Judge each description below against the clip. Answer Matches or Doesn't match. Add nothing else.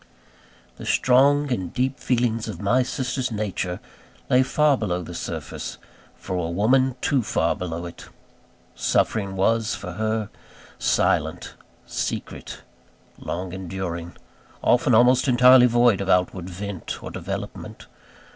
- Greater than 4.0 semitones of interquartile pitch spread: Matches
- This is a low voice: Matches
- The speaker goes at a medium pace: Doesn't match